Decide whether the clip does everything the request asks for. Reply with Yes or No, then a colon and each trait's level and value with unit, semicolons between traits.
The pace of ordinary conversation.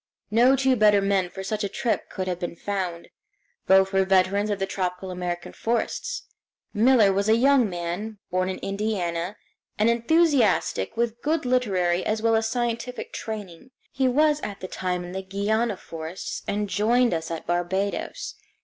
Yes: average, 165 wpm